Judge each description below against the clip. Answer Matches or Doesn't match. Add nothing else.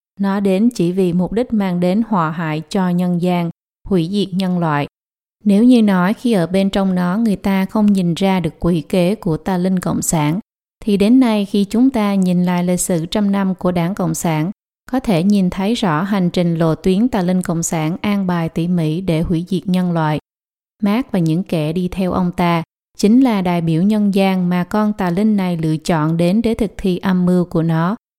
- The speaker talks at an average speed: Doesn't match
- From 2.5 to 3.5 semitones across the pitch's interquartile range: Matches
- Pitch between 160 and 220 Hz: Matches